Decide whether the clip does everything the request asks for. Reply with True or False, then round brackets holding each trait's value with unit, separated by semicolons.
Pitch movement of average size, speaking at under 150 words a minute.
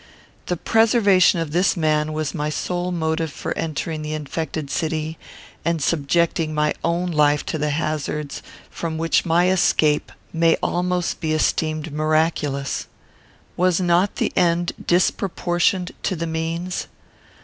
False (2.2 semitones; 135 wpm)